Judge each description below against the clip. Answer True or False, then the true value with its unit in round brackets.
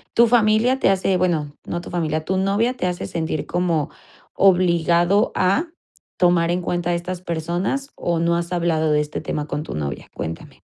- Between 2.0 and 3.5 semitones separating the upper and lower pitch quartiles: True (2.6 semitones)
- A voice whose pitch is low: False (175 Hz)